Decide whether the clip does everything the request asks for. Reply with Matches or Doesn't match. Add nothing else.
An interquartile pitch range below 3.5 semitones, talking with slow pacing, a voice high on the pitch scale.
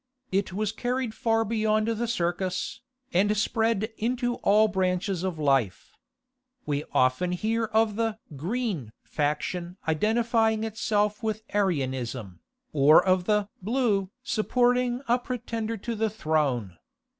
Doesn't match